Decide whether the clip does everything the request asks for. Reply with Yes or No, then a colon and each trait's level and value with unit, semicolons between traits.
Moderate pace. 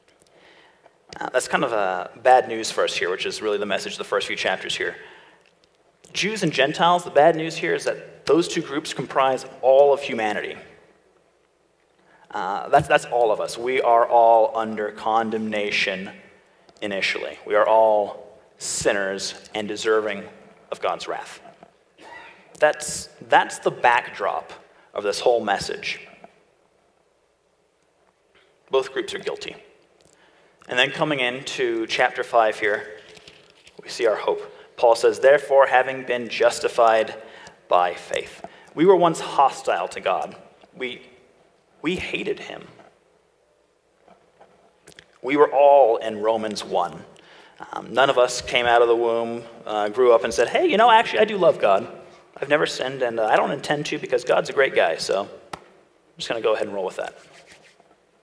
Yes: average, 160 wpm